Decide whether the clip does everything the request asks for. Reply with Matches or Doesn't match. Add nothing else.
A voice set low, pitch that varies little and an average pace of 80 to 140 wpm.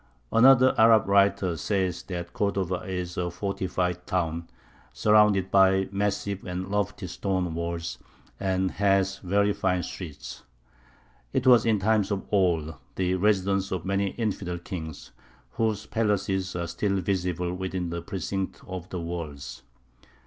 Matches